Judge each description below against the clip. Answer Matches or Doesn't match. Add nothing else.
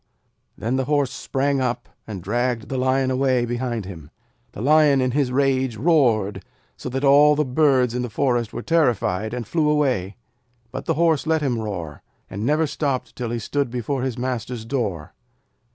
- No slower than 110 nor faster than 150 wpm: Doesn't match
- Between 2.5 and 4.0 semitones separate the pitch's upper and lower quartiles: Matches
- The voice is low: Matches